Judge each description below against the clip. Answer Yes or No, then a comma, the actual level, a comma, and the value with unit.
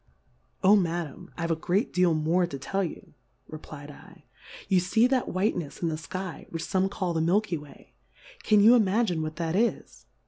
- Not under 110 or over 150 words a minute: No, average, 185 wpm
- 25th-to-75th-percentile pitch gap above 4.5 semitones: No, average, 3.5 semitones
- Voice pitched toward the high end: No, medium, 180 Hz